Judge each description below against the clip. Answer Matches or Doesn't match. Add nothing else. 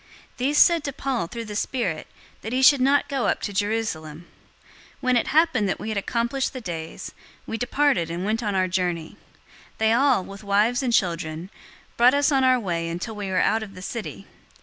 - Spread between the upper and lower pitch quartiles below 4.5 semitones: Doesn't match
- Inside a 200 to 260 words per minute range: Matches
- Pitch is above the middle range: Matches